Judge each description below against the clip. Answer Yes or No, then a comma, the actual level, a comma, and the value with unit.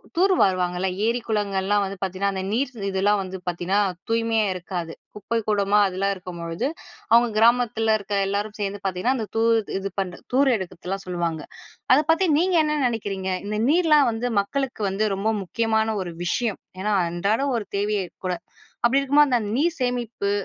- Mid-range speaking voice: No, high, 210 Hz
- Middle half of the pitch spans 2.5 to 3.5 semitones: No, average, 3.9 semitones